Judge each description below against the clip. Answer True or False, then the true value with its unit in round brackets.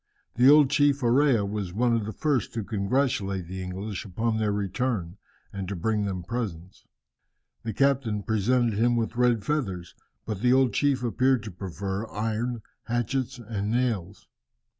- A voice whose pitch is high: False (110 Hz)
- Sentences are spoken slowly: False (160 wpm)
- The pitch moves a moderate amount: True (3.9 semitones)